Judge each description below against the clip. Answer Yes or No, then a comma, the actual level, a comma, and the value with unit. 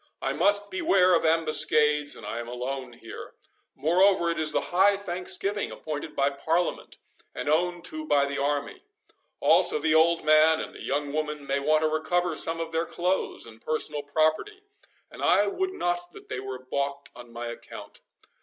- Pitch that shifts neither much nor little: Yes, average, 3.9 semitones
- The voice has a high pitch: No, medium, 155 Hz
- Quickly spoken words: No, average, 175 wpm